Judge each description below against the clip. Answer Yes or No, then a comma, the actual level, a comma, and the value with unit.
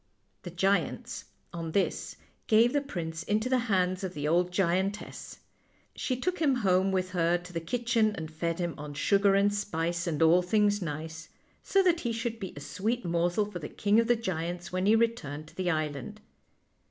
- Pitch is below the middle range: No, medium, 185 Hz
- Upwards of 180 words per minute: Yes, average, 190 wpm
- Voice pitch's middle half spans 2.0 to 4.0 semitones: No, average, 4.4 semitones